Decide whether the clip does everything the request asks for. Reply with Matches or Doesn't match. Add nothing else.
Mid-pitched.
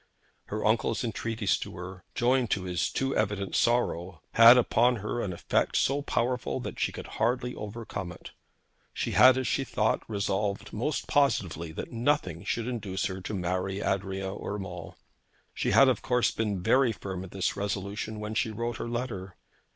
Doesn't match